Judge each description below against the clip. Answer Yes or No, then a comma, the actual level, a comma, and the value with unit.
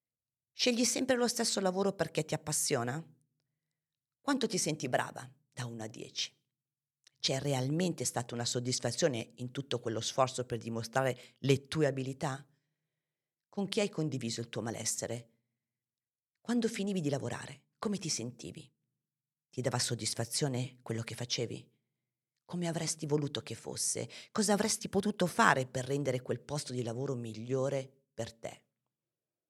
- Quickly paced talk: No, average, 140 wpm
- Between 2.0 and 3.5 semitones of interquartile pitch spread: No, average, 4.4 semitones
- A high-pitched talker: No, low, 135 Hz